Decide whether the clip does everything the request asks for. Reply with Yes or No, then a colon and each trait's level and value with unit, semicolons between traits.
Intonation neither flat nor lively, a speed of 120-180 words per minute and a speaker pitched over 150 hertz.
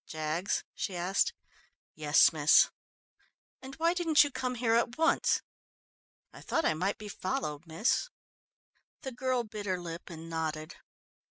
No: wide, 7.7 semitones; average, 145 wpm; high, 190 Hz